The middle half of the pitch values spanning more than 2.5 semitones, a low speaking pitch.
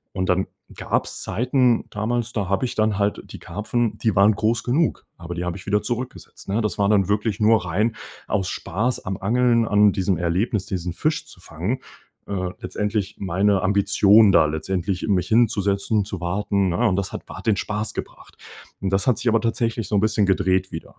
Yes: average, 2.9 semitones; low, 100 Hz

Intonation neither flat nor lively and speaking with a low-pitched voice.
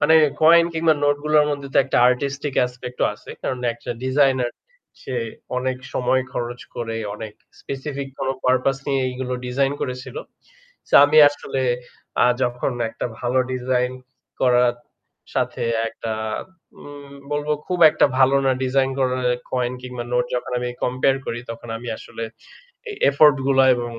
No: narrow, 2.0 semitones; low, 130 Hz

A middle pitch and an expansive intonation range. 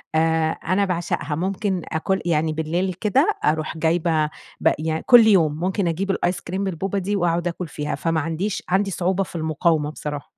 No: medium, 170 Hz; average, 3.1 semitones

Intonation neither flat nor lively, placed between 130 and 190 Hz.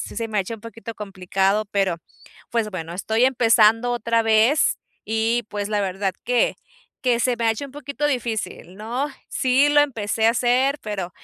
No: average, 3.0 semitones; high, 225 Hz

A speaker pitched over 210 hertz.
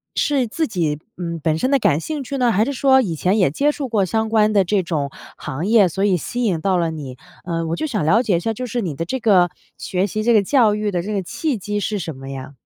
No: high, 200 Hz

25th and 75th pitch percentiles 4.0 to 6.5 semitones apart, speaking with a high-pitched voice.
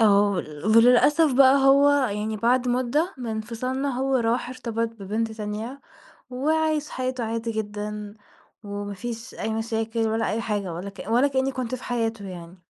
No: average, 3.4 semitones; high, 230 Hz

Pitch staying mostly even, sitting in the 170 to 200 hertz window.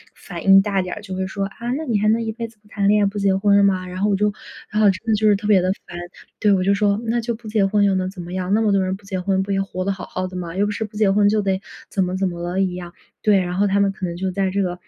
Yes: narrow, 2.0 semitones; high, 195 Hz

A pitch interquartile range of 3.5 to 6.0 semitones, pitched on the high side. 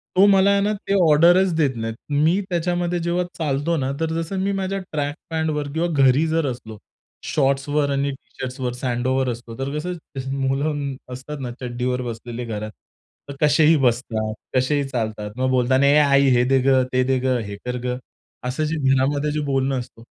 No: average, 3.8 semitones; low, 135 Hz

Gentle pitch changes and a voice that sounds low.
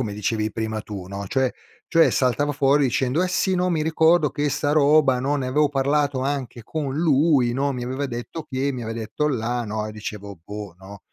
No: average, 4.7 semitones; low, 130 Hz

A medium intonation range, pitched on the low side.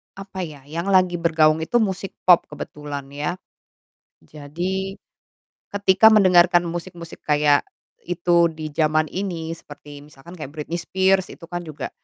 No: average, 3.5 semitones; medium, 170 Hz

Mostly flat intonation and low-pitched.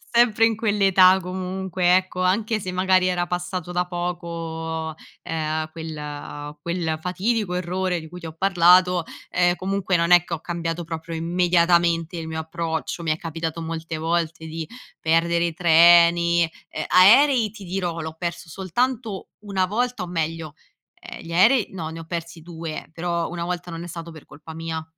No: narrow, 2.1 semitones; medium, 170 Hz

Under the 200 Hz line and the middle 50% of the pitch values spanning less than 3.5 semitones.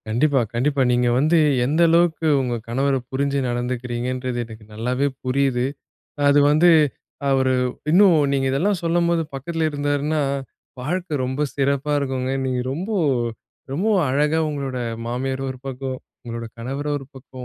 Yes: low, 135 Hz; average, 3.0 semitones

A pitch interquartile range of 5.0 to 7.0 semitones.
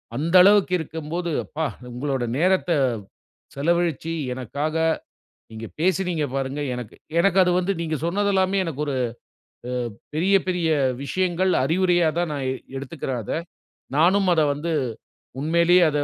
No: average, 3.9 semitones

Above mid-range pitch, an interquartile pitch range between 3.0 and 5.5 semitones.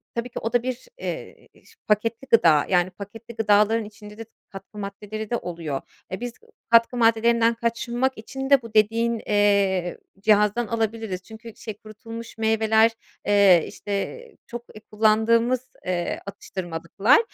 No: high, 220 Hz; narrow, 2.4 semitones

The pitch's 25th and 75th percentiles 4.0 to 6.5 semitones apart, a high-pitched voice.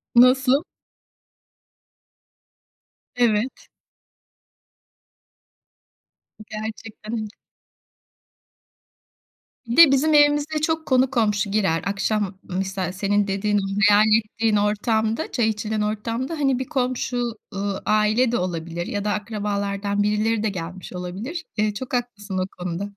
No: average, 3.6 semitones; high, 215 Hz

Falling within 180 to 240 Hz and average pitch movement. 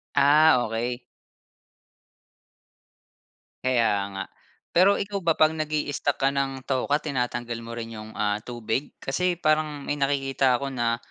No: low, 135 Hz; average, 4.1 semitones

